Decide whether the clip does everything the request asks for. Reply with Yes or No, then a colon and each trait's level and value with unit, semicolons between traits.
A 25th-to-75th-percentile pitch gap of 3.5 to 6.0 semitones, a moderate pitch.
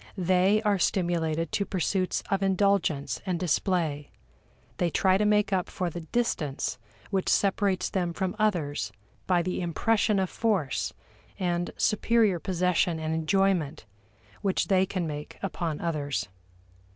No: average, 3.1 semitones; medium, 180 Hz